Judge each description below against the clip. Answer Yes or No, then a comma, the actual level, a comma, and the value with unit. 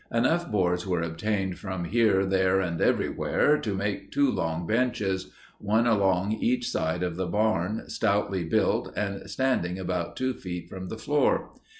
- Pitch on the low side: Yes, very low, 95 Hz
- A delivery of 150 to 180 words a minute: Yes, average, 160 wpm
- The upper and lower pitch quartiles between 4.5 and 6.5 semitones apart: No, average, 3.8 semitones